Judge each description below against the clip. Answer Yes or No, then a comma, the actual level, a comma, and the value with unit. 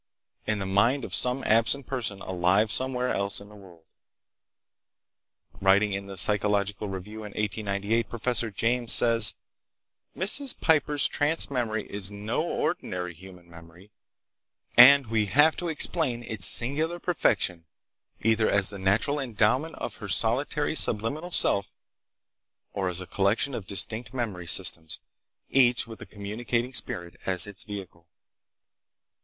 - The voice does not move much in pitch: No, average, 4.2 semitones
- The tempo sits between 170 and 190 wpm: No, slow, 135 wpm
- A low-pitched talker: Yes, low, 110 Hz